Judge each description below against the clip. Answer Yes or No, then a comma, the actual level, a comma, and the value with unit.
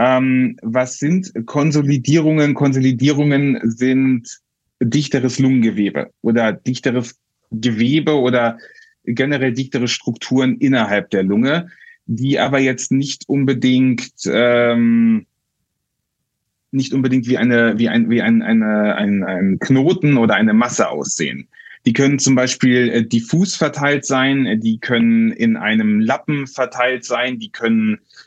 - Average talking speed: No, slow, 115 wpm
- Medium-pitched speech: No, low, 130 Hz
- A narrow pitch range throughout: No, average, 3.3 semitones